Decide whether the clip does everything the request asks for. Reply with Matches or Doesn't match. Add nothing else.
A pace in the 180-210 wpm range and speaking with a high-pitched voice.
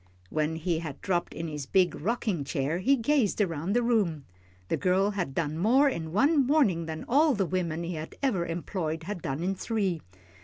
Doesn't match